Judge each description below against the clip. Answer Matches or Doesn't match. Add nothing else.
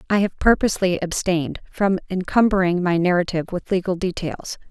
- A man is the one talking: Doesn't match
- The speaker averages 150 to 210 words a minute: Doesn't match